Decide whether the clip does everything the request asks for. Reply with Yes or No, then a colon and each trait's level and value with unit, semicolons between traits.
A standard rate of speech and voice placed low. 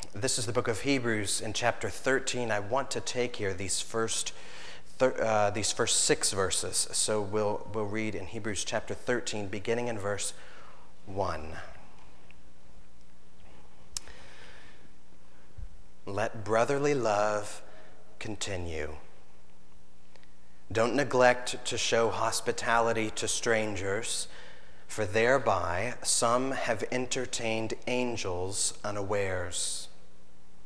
No: slow, 100 wpm; low, 105 Hz